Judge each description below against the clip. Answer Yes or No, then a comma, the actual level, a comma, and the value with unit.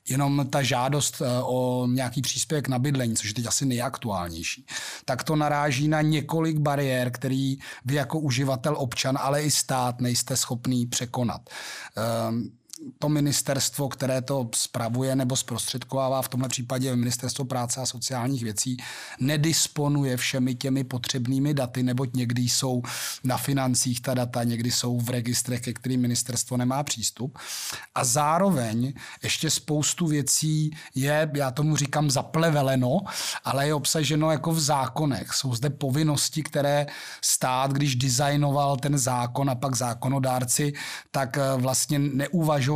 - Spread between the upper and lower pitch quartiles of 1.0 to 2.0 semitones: No, narrow, 2.5 semitones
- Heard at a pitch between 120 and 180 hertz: Yes, low, 135 Hz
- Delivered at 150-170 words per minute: No, average, 140 wpm